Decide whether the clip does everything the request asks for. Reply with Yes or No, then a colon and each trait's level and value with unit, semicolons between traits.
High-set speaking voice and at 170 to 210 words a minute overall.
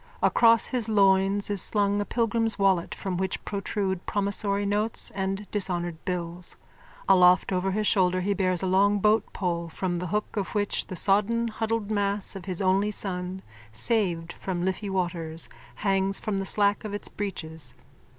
No: high, 195 Hz; average, 160 wpm